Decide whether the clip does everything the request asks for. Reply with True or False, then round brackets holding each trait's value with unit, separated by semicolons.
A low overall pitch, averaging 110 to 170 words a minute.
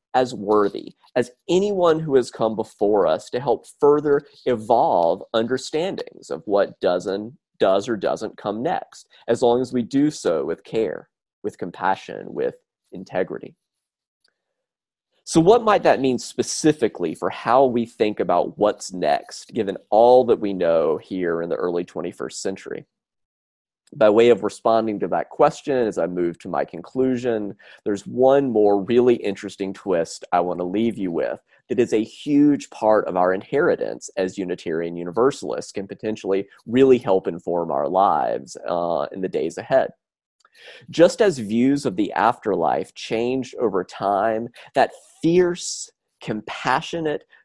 True (120 Hz; 150 wpm)